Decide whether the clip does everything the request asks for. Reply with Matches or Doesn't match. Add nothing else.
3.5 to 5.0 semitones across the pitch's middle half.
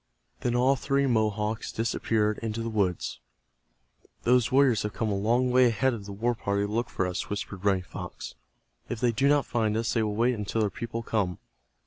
Doesn't match